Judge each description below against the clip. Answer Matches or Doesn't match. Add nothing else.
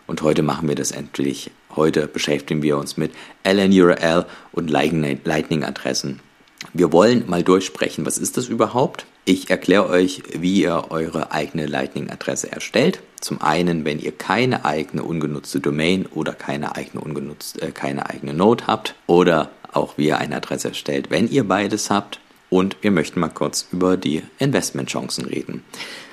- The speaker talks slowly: Doesn't match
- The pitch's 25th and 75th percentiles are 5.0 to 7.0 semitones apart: Doesn't match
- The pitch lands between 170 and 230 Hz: Doesn't match